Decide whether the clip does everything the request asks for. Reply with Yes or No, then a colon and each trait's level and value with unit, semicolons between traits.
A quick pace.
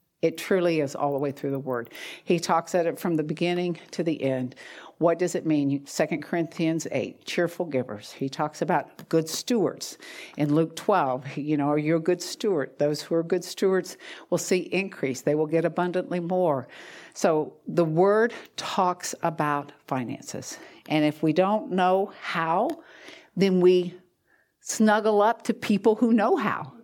No: average, 170 wpm